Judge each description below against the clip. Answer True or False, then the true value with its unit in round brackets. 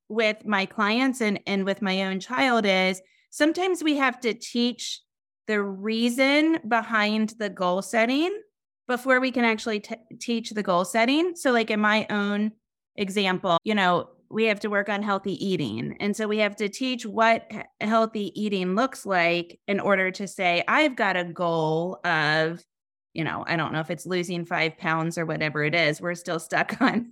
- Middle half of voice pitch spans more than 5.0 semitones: False (3.9 semitones)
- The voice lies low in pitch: False (210 Hz)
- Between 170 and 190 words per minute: True (185 wpm)